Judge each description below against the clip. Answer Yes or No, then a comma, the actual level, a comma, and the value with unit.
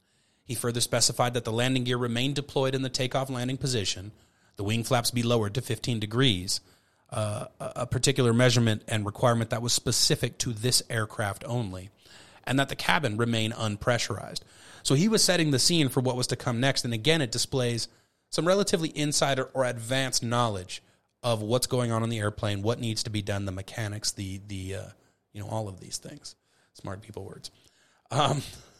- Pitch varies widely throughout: No, average, 3.2 semitones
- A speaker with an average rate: Yes, average, 190 wpm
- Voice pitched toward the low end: Yes, low, 120 Hz